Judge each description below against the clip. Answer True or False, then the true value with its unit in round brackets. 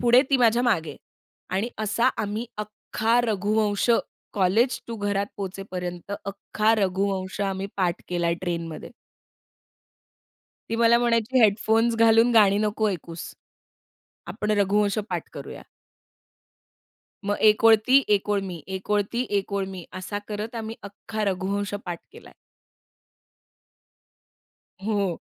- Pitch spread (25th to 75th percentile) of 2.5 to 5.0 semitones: True (2.8 semitones)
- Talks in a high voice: True (205 Hz)